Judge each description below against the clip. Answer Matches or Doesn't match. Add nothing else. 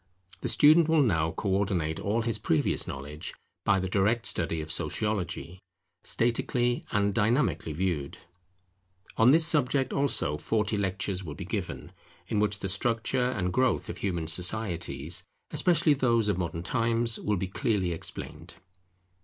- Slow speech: Doesn't match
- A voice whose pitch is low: Matches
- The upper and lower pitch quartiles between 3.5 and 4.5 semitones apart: Doesn't match